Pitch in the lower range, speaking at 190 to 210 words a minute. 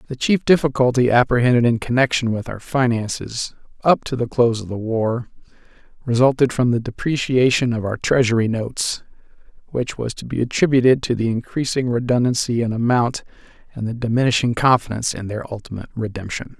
No: low, 120 Hz; average, 155 wpm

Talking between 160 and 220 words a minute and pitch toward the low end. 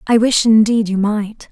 No: average, 200 wpm; high, 215 Hz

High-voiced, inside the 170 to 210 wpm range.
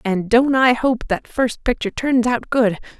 Yes: high, 235 Hz; average, 200 wpm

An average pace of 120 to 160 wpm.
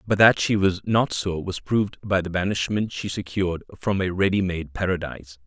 No: average, 200 wpm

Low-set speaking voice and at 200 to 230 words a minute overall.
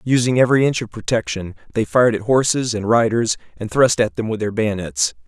Yes: low, 110 Hz; fast, 205 wpm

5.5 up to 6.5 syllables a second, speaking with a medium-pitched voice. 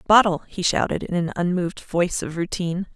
Yes: 6.0 syllables/s; medium, 180 Hz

